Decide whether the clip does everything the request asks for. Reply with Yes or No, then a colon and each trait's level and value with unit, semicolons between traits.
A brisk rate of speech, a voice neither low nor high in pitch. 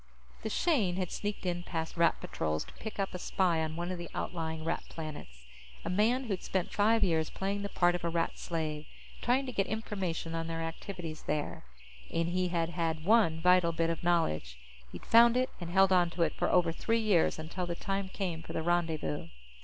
Yes: fast, 210 wpm; medium, 175 Hz